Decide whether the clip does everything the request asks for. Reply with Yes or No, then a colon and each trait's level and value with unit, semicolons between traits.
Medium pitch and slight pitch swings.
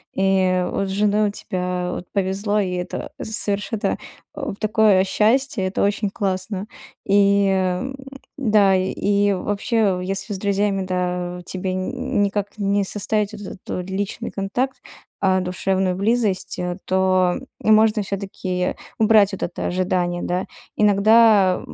No: high, 195 Hz; narrow, 1.9 semitones